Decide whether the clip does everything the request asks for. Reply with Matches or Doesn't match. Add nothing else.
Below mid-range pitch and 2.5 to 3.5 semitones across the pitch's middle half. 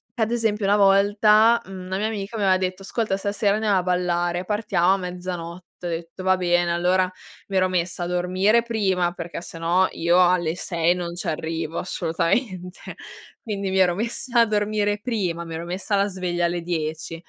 Doesn't match